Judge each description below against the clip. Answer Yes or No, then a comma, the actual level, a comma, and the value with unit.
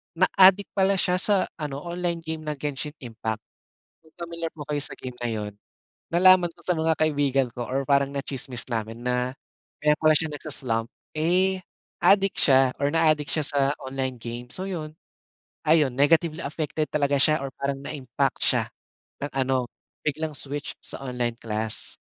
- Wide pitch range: No, average, 3.7 semitones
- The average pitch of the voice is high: No, medium, 145 Hz